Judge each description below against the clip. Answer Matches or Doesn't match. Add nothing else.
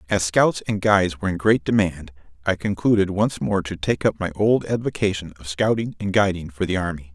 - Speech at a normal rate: Doesn't match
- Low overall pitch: Matches